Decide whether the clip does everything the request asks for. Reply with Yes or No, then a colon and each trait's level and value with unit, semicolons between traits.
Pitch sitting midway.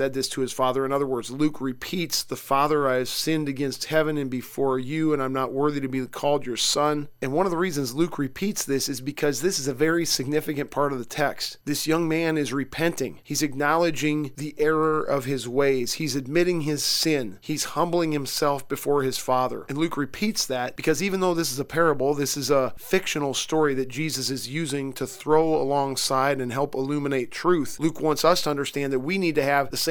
Yes: medium, 145 Hz